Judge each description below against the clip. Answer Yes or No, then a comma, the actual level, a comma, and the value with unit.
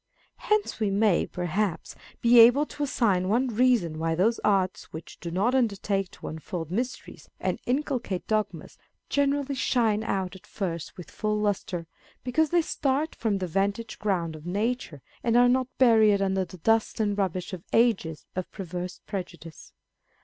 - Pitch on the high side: Yes, high, 205 Hz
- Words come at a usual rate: Yes, average, 160 wpm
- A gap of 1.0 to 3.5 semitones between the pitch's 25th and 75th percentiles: No, average, 5.0 semitones